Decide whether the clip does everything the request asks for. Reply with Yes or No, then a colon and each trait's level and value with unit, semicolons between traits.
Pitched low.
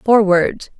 No: high, 205 Hz